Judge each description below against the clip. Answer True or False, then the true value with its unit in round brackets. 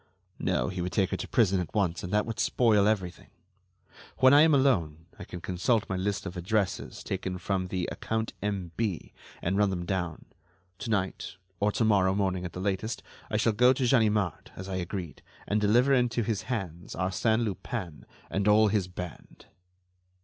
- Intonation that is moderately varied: True (3.2 semitones)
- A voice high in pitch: False (100 Hz)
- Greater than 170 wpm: True (185 wpm)